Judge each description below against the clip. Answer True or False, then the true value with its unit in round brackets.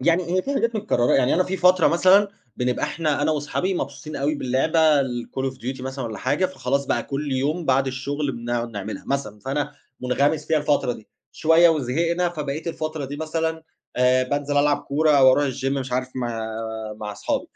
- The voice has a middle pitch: True (145 Hz)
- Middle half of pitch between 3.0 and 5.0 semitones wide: True (3.8 semitones)